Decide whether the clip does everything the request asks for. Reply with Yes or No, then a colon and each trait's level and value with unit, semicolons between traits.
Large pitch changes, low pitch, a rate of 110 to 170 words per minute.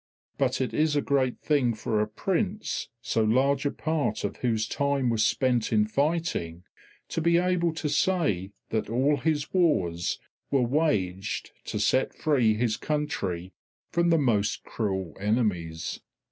Yes: wide, 6.0 semitones; low, 125 Hz; average, 150 wpm